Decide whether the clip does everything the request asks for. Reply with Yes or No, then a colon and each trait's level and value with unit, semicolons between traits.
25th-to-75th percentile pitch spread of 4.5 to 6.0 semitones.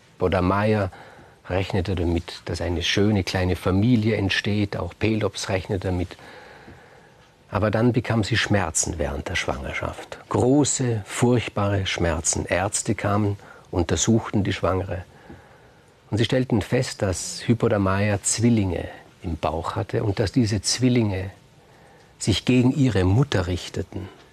No: average, 3.8 semitones